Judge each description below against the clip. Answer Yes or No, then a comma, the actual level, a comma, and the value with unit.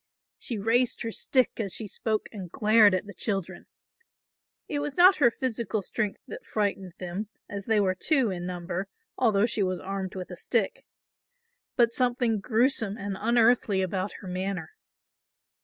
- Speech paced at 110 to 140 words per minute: No, average, 160 wpm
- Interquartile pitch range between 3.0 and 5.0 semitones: Yes, average, 3.7 semitones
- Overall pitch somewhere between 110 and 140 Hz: No, high, 210 Hz